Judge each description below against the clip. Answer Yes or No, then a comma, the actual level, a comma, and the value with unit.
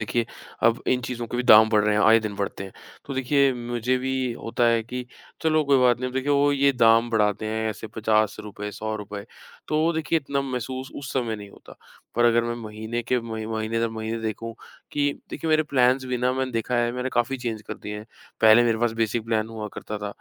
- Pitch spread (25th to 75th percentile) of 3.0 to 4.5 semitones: No, narrow, 2.6 semitones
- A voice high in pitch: No, low, 115 Hz